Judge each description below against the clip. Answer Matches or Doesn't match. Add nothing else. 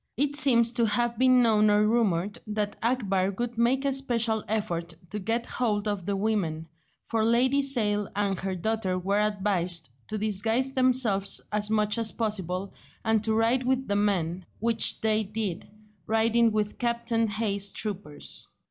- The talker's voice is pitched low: Doesn't match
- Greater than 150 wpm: Matches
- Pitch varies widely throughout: Doesn't match